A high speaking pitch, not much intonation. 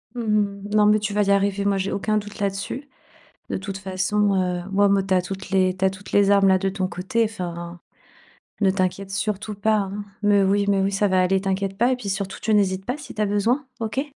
Yes: high, 200 Hz; narrow, 1.6 semitones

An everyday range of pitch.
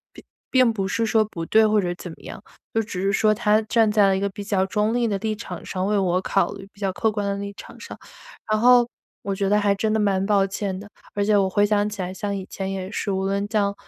No: narrow, 1.7 semitones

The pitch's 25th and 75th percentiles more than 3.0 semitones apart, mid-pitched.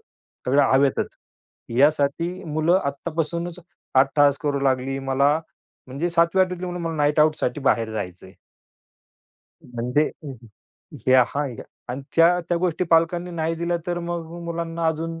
Yes: average, 3.8 semitones; medium, 155 Hz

